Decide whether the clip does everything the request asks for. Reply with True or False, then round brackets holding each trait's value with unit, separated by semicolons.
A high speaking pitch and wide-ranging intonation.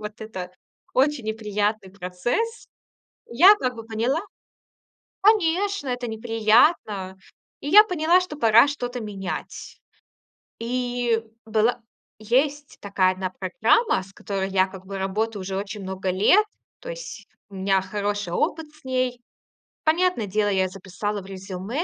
True (220 Hz; 5.8 semitones)